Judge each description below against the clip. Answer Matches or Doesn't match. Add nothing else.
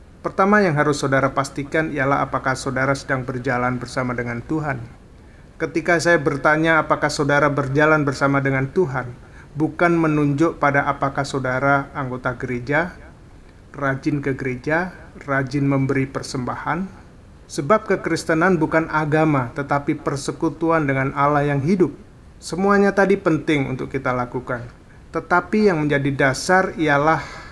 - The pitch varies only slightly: Doesn't match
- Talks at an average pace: Matches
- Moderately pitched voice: Matches